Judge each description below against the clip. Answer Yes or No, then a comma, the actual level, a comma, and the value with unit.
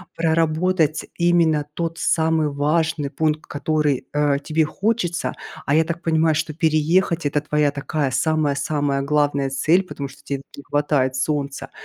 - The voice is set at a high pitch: No, medium, 155 Hz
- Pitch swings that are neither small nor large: No, narrow, 2.1 semitones